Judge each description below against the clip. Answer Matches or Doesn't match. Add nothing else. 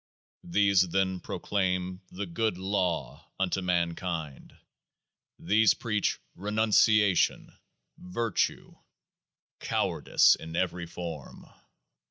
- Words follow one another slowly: Matches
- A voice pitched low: Matches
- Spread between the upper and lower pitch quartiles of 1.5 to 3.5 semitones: Matches